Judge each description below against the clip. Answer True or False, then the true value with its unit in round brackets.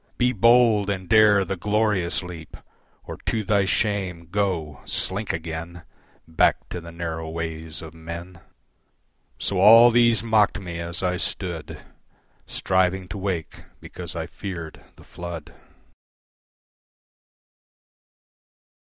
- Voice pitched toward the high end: False (90 Hz)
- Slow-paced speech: True (120 wpm)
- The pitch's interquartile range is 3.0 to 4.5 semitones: True (3.5 semitones)